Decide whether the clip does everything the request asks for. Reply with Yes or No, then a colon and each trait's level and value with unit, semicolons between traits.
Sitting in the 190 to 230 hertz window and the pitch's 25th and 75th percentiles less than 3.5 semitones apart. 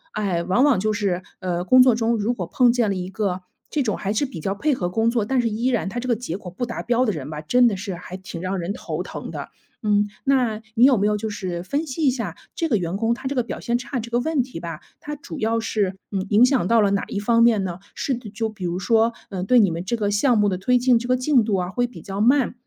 No: high, 220 Hz; average, 4.3 semitones